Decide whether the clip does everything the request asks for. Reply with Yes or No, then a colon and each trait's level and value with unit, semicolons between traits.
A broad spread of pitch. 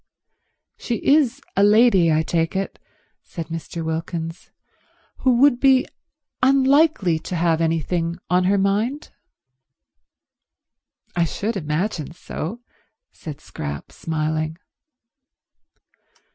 Yes: wide, 6.5 semitones